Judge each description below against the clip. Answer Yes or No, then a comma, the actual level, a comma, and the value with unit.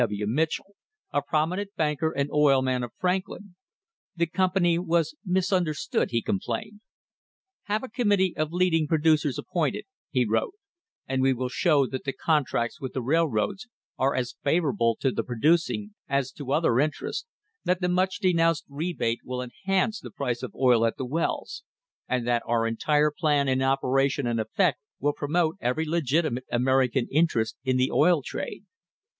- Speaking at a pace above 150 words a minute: Yes, average, 160 wpm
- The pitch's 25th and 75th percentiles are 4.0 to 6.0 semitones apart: Yes, average, 5.1 semitones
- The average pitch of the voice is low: No, medium, 150 Hz